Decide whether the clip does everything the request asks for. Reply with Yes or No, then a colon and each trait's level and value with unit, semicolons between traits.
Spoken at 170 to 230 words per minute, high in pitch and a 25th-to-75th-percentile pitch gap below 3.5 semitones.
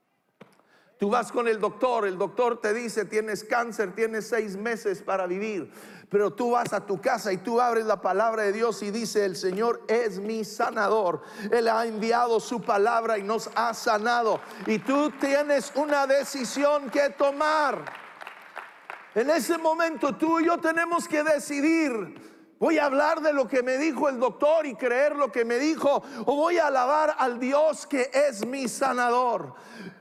No: average, 175 wpm; high, 245 Hz; average, 4.6 semitones